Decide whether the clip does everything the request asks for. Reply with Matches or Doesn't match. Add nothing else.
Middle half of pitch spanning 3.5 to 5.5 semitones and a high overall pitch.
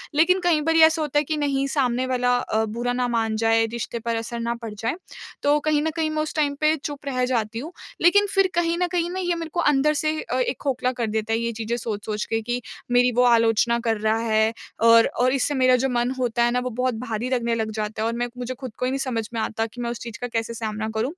Matches